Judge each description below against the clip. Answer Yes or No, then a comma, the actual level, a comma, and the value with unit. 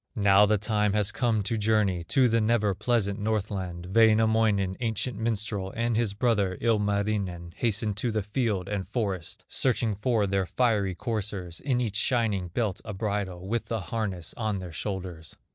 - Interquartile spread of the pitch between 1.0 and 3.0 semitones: Yes, average, 2.7 semitones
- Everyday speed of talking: Yes, average, 160 wpm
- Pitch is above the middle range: No, low, 105 Hz